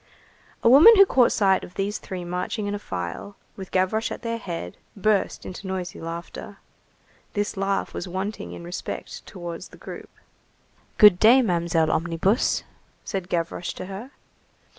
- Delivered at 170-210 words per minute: No, average, 155 wpm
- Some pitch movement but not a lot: Yes, average, 3.2 semitones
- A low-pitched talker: No, high, 190 Hz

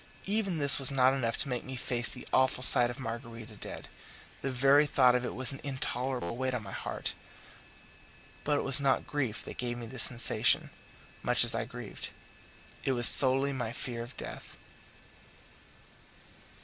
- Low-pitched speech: Yes, low, 130 Hz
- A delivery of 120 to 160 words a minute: No, average, 175 wpm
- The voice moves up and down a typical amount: No, narrow, 2.2 semitones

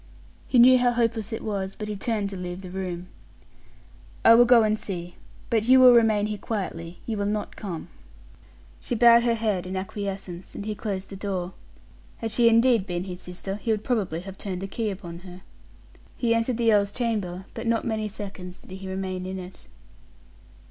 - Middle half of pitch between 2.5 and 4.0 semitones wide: Yes, average, 3.4 semitones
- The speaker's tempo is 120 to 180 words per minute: No, average, 195 wpm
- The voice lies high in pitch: Yes, high, 205 Hz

